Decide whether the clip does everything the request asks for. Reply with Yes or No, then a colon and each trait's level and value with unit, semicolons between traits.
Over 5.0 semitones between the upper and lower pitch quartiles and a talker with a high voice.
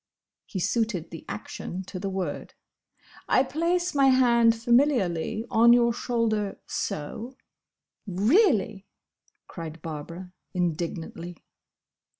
Yes: wide, 5.5 semitones; high, 210 Hz